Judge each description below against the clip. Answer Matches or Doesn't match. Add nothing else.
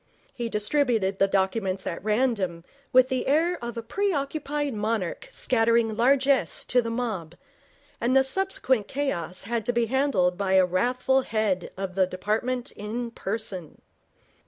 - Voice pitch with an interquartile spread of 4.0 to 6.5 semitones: Matches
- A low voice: Doesn't match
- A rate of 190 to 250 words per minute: Doesn't match